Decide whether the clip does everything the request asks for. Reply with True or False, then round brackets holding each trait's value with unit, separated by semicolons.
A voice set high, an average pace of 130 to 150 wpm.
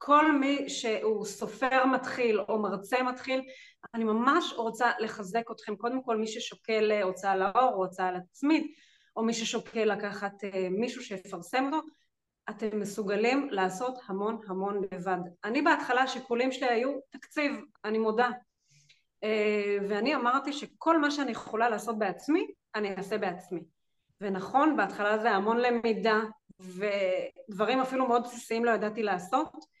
True (225 Hz; 135 wpm)